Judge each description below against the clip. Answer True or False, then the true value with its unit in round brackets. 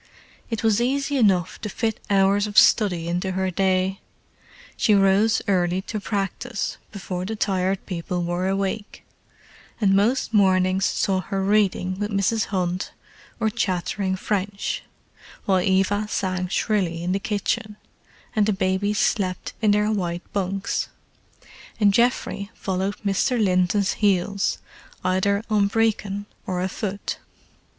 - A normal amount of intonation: False (2.0 semitones)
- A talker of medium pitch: False (195 Hz)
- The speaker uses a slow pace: True (130 wpm)